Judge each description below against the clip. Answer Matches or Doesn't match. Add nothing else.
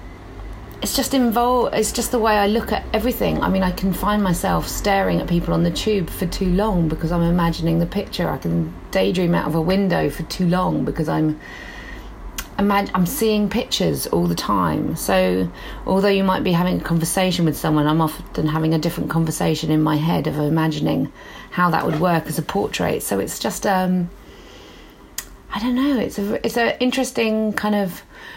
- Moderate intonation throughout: Matches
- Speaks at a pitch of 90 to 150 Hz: Doesn't match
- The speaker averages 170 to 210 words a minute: Matches